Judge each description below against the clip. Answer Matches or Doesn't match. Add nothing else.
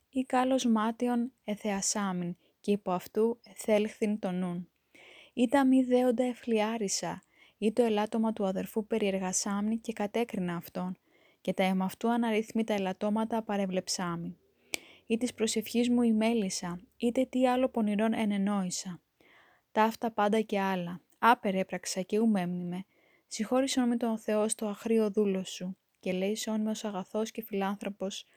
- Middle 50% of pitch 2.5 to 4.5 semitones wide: Matches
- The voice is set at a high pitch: Matches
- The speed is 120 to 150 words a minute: Matches